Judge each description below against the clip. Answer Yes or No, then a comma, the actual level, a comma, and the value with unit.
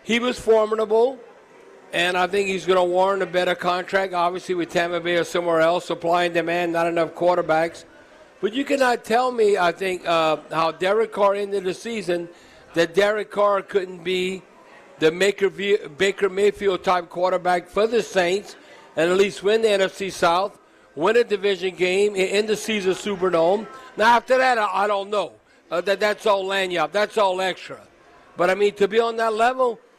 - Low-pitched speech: No, high, 195 Hz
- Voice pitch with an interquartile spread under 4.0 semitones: Yes, average, 2.9 semitones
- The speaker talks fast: No, average, 180 wpm